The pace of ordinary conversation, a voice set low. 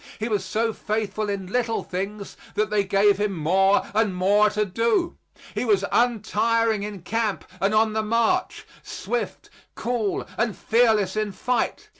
No: average, 155 wpm; high, 210 Hz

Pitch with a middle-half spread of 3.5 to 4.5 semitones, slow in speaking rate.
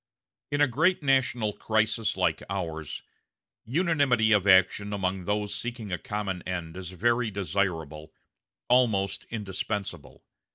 Yes: average, 4.2 semitones; slow, 120 wpm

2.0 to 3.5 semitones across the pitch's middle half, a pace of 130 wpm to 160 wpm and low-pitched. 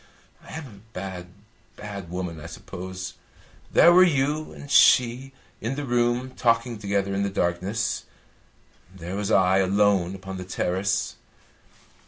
No: average, 4.5 semitones; average, 140 wpm; low, 100 Hz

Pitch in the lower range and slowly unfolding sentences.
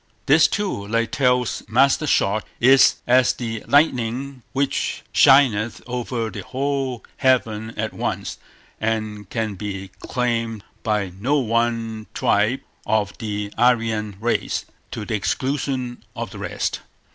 Yes: low, 115 Hz; slow, 125 wpm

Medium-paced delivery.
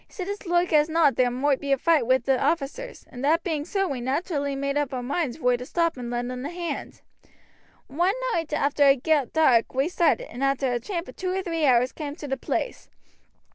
No: fast, 235 wpm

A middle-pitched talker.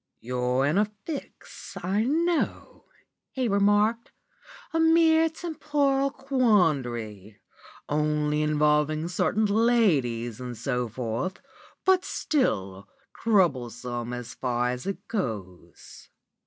Yes: medium, 155 Hz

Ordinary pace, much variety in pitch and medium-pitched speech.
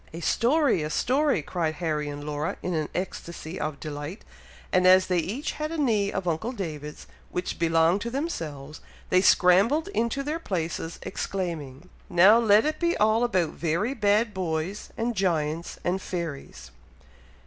Yes: average, 160 wpm; wide, 6.0 semitones; medium, 180 Hz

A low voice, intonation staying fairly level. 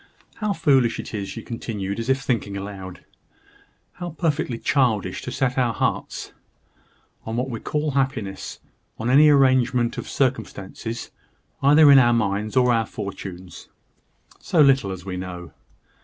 No: low, 120 Hz; average, 5.0 semitones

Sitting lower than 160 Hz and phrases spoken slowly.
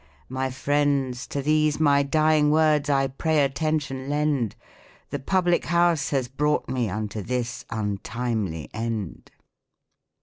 Yes: medium, 140 Hz; slow, 130 wpm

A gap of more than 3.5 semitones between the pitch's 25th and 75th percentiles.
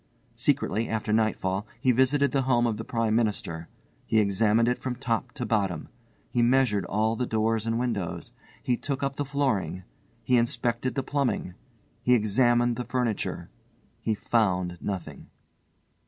No: average, 2.9 semitones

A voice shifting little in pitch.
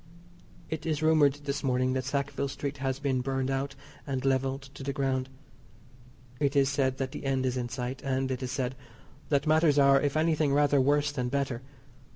Yes: narrow, 1.5 semitones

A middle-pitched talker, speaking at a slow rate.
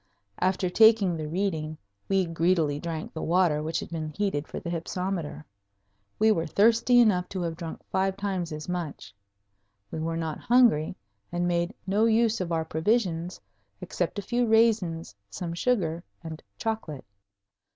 No: medium, 175 Hz; average, 155 wpm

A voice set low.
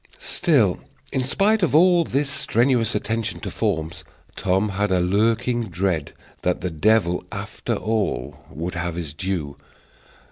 Yes: low, 105 Hz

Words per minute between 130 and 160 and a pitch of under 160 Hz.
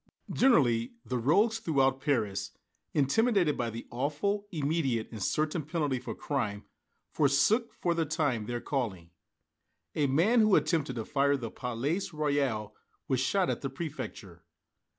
Yes: average, 140 wpm; medium, 140 Hz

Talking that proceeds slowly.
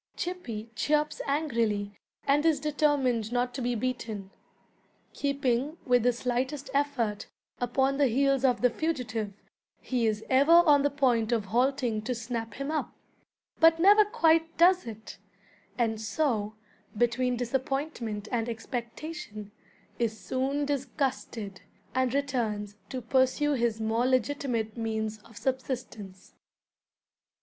Yes: slow, 125 wpm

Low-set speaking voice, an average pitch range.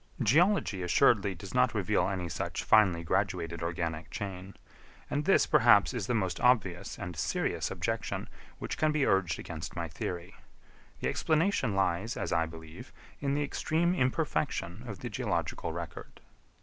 No: low, 100 Hz; wide, 6.9 semitones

